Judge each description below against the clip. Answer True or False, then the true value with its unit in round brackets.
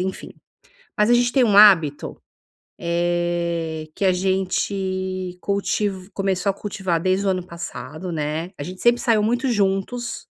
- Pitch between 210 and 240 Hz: False (185 Hz)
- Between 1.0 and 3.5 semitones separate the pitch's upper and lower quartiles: True (2.8 semitones)